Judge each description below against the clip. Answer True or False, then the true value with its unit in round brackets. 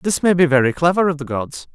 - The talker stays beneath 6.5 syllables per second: True (6.2 syllables/s)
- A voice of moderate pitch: True (155 Hz)